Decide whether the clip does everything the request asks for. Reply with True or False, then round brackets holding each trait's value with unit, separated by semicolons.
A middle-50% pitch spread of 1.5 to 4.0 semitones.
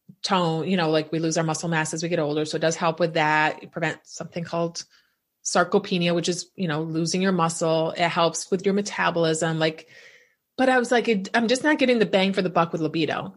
True (3.2 semitones)